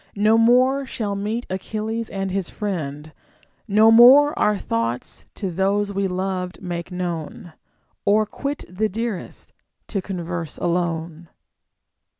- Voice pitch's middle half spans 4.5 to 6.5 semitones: No, average, 3.9 semitones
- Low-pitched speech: No, high, 195 Hz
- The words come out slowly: Yes, slow, 130 wpm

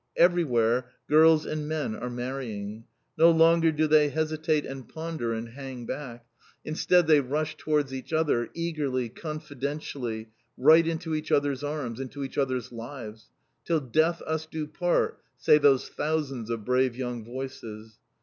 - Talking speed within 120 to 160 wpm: Yes, average, 150 wpm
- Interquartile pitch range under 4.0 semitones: No, average, 4.3 semitones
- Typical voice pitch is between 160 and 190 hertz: No, medium, 140 Hz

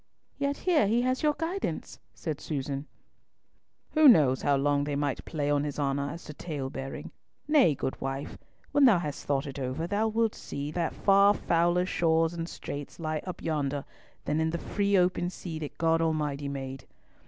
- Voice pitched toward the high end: No, medium, 160 Hz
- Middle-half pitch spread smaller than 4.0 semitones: No, wide, 5.6 semitones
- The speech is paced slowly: No, average, 175 wpm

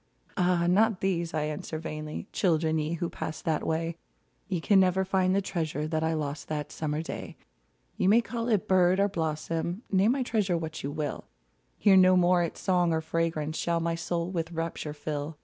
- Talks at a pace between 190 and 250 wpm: Yes, average, 195 wpm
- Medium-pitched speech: Yes, medium, 170 Hz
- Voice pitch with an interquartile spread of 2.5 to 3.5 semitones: Yes, average, 3.0 semitones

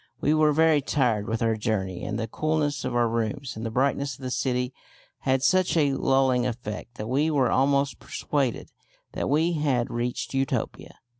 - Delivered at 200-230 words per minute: No, average, 180 wpm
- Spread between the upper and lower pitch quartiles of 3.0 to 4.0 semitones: Yes, average, 3.4 semitones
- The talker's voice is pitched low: Yes, low, 130 Hz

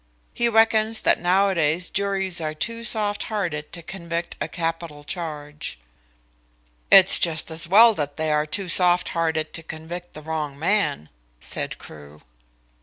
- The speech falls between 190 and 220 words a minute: No, average, 150 wpm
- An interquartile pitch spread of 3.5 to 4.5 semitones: Yes, average, 4.0 semitones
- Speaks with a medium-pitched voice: Yes, medium, 170 Hz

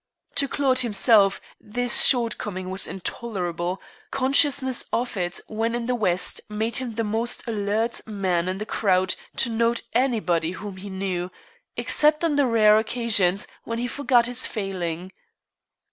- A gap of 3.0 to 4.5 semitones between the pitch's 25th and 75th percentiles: Yes, average, 4.2 semitones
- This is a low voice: No, high, 220 Hz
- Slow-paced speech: No, average, 150 wpm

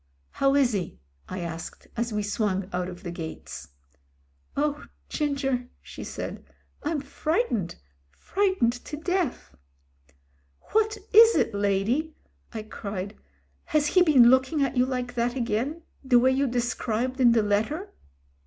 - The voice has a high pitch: Yes, high, 245 Hz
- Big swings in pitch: Yes, wide, 5.9 semitones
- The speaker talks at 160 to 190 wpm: No, average, 150 wpm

